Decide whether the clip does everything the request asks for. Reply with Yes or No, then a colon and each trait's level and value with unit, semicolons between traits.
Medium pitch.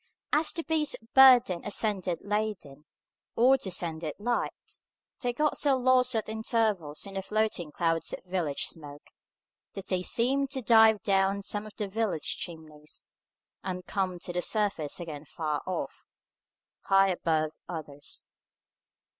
No: high, 195 Hz